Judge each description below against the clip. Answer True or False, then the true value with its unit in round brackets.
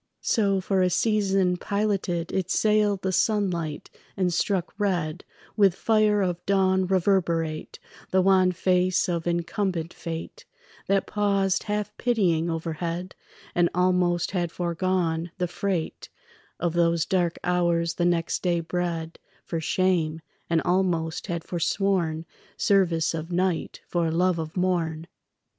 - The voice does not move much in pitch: True (2.3 semitones)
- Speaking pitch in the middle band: True (180 Hz)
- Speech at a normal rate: False (130 wpm)